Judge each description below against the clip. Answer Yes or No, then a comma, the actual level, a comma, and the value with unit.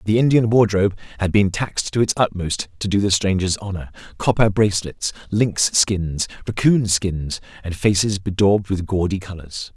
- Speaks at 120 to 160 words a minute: Yes, average, 155 wpm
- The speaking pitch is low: Yes, low, 100 Hz